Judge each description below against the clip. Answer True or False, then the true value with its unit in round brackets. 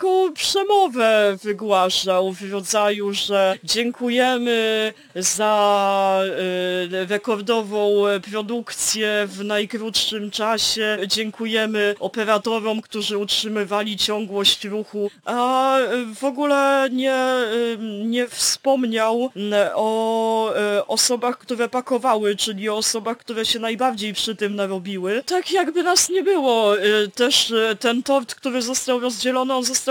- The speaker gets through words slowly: True (100 wpm)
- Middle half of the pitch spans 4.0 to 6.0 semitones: False (3.2 semitones)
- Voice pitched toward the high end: True (220 Hz)